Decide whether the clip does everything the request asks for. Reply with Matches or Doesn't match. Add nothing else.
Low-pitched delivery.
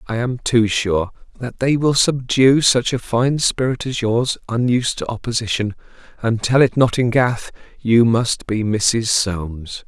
Matches